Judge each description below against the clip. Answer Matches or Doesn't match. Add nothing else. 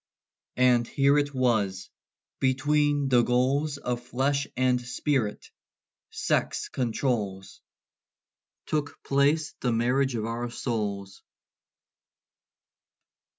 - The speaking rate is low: Matches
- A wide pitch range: Doesn't match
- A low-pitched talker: Matches